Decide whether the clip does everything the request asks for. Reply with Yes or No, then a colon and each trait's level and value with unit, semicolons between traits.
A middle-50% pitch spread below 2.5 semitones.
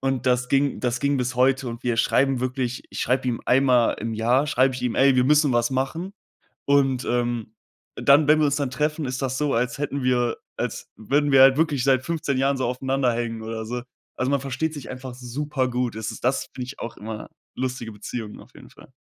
Yes: narrow, 2.1 semitones